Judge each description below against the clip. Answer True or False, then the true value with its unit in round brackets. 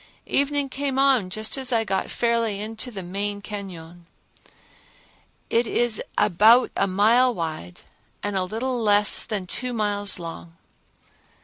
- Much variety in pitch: False (3.9 semitones)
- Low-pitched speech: False (210 Hz)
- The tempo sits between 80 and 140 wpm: True (135 wpm)